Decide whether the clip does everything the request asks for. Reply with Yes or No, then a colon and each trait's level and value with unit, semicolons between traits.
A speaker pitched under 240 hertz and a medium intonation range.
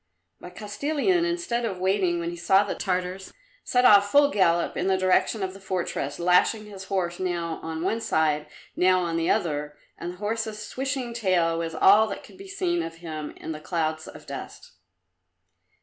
Yes: medium, 185 Hz; average, 4.5 semitones